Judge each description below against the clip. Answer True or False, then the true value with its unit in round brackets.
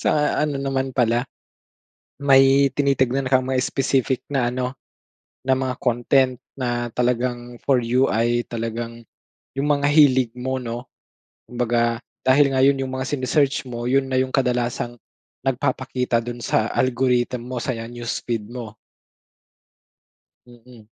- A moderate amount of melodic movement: False (1.8 semitones)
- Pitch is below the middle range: True (125 Hz)